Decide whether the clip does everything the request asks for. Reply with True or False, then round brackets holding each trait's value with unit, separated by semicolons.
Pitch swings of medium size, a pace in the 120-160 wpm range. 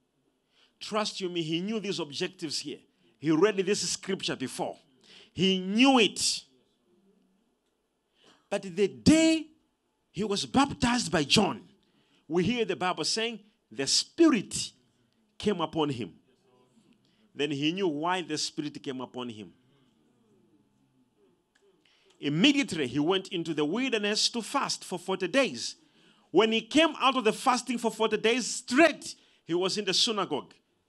False (6.3 semitones; 135 wpm)